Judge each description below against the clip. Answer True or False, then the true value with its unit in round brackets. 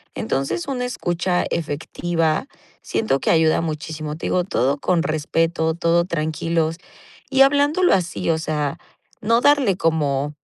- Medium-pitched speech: True (165 Hz)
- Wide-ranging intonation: False (3.0 semitones)